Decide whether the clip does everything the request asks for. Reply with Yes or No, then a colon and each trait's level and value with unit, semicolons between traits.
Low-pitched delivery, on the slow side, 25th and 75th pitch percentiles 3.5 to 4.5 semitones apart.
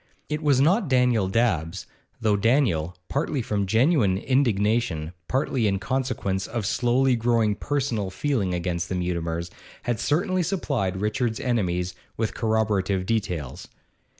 No: low, 110 Hz; slow, 125 wpm; wide, 5.6 semitones